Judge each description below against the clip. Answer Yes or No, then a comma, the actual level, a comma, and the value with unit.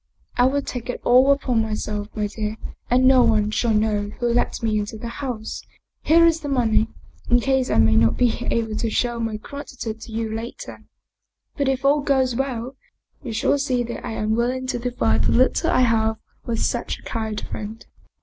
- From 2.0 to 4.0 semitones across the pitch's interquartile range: Yes, average, 2.9 semitones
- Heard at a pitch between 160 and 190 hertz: No, high, 235 Hz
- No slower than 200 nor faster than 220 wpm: Yes, fast, 205 wpm